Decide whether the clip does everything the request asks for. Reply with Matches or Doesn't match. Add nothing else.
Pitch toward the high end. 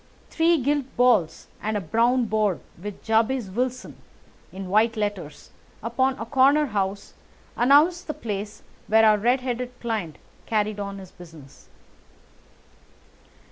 Matches